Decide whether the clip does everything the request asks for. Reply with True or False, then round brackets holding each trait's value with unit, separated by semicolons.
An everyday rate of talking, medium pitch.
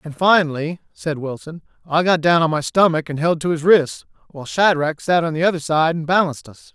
False (220 wpm; 160 Hz)